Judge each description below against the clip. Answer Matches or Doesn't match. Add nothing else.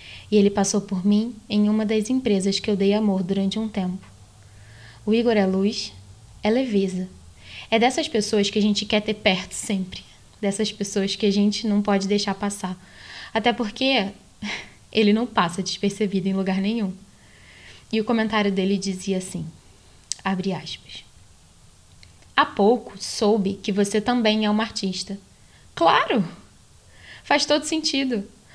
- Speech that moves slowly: Doesn't match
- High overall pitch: Matches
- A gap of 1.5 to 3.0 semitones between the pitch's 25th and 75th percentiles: Matches